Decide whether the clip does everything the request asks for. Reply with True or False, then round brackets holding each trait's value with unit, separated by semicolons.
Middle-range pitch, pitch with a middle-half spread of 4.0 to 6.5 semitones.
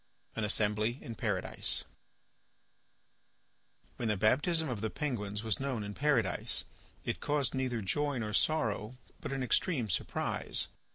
False (115 Hz; 4.6 semitones)